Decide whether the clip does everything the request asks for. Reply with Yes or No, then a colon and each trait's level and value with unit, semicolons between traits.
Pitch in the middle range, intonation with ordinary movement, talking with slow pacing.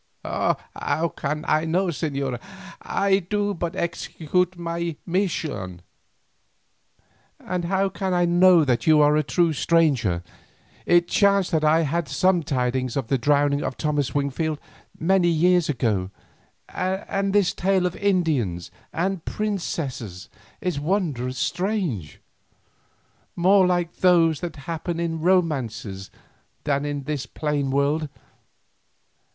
Yes: medium, 165 Hz; average, 4.4 semitones; slow, 125 wpm